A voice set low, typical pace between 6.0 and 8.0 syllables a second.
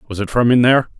Yes: low, 120 Hz; 6.7 syllables/s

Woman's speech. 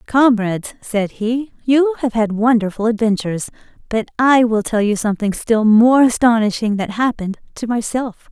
Yes: female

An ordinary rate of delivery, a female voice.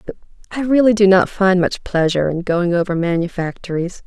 Yes: average, 175 wpm; female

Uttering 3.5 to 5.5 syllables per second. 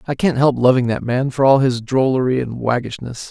Yes: 5.4 syllables/s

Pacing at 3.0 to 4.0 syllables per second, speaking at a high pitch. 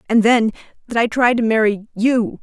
No: 5.1 syllables/s; high, 225 Hz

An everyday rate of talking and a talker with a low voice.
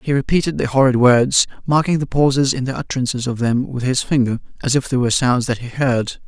No: fast, 220 wpm; low, 130 Hz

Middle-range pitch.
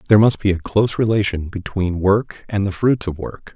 No: low, 100 Hz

